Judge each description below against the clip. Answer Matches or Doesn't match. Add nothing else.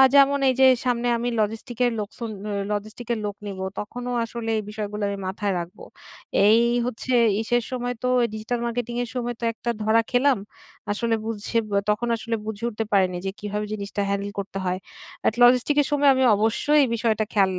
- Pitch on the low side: Doesn't match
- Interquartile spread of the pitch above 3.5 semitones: Doesn't match